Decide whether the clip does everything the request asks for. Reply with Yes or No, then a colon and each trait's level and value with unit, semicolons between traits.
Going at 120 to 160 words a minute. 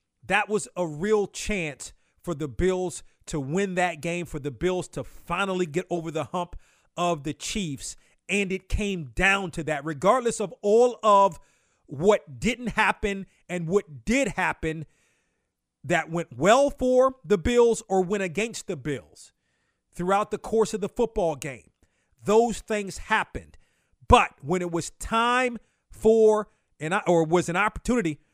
Yes: average, 155 wpm